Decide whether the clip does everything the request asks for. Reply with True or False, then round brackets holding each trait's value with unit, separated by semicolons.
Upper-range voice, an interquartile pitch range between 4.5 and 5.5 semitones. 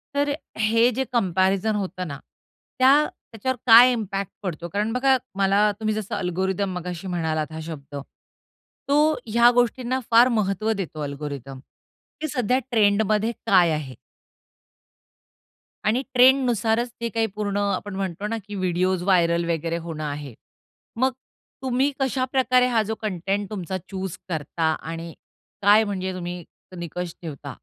True (200 Hz; 5.1 semitones)